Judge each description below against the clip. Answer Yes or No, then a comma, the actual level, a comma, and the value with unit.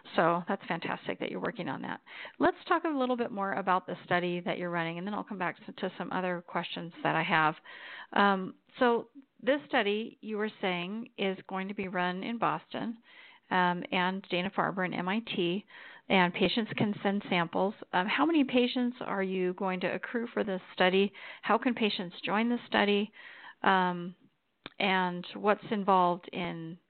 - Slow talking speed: No, average, 180 wpm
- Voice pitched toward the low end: No, high, 195 Hz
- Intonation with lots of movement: No, average, 3.6 semitones